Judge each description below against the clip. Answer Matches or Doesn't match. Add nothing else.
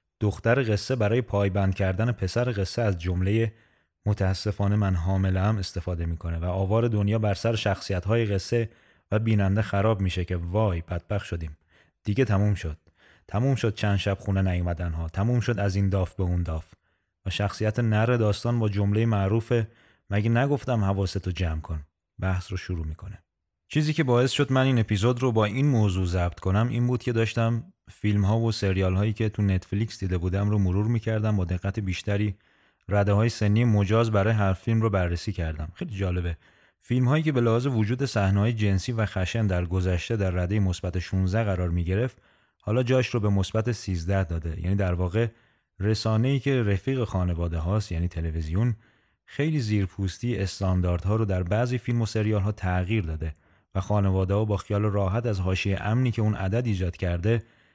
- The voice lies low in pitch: Matches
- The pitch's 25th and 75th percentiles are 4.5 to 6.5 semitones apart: Doesn't match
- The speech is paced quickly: Matches